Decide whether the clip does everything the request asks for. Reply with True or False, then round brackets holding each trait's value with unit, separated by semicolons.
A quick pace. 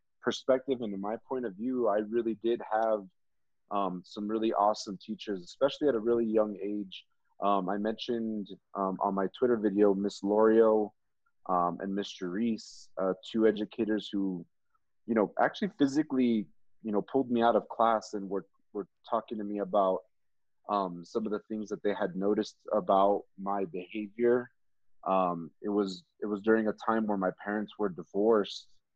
False (170 wpm)